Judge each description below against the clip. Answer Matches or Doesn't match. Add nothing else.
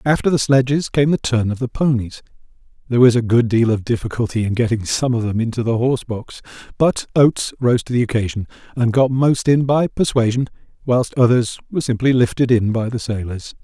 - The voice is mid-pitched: Doesn't match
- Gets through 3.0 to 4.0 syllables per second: Doesn't match